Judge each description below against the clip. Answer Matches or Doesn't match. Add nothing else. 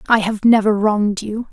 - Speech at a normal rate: Matches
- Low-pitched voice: Doesn't match